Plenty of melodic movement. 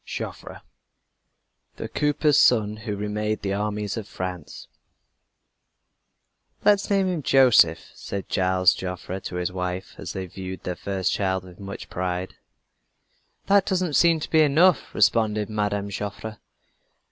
Yes: wide, 6.3 semitones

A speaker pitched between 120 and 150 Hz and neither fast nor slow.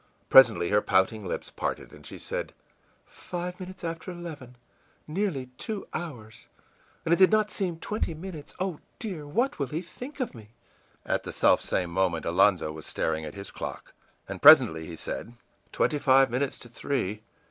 Yes: medium, 140 Hz; average, 170 wpm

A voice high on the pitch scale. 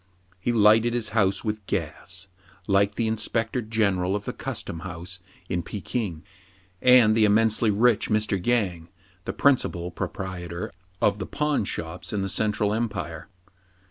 No: low, 105 Hz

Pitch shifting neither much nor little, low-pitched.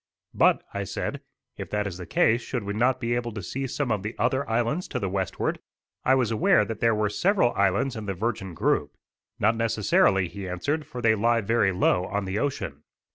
Yes: average, 3.6 semitones; low, 110 Hz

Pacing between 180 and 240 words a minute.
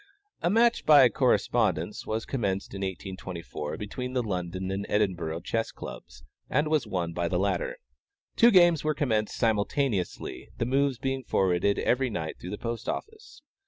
No: average, 160 wpm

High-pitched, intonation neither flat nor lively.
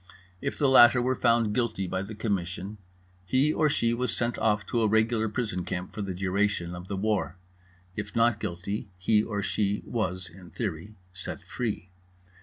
No: low, 105 Hz; average, 3.8 semitones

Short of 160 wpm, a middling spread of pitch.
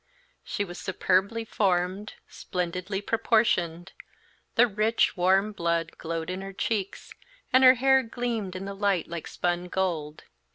Yes: slow, 135 wpm; average, 3.6 semitones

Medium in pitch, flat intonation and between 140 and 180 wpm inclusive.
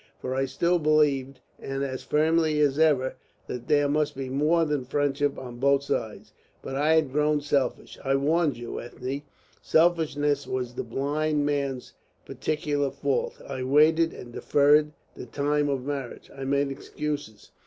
Yes: medium, 145 Hz; narrow, 2.0 semitones; average, 155 wpm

